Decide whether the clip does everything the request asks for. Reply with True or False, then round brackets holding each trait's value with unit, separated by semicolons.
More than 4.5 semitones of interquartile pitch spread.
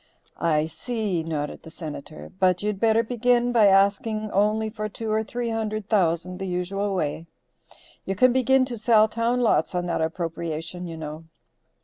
True (5.0 semitones)